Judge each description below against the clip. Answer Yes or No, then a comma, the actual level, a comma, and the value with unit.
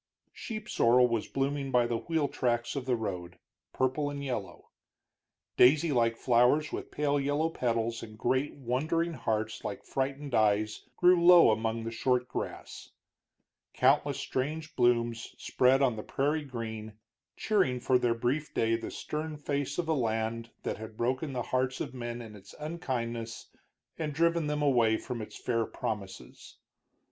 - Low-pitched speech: Yes, low, 125 Hz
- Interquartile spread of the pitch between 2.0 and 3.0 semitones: No, average, 4.0 semitones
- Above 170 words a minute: No, average, 155 wpm